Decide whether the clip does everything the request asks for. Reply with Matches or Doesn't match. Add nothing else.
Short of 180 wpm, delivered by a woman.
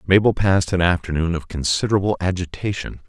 Doesn't match